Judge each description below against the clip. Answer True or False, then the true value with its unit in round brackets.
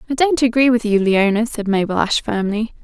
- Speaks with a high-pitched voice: True (225 Hz)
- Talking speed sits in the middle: False (210 wpm)